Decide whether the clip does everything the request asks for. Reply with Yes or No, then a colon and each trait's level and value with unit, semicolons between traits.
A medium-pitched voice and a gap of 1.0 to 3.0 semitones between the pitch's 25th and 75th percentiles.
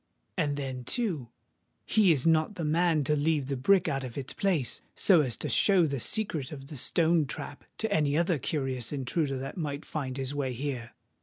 No: medium, 145 Hz; average, 3.8 semitones